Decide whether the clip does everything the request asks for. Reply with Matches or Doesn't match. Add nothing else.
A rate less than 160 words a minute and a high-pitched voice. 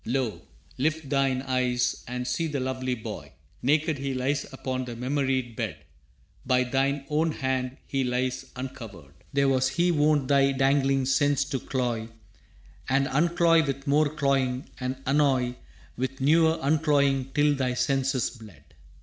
Doesn't match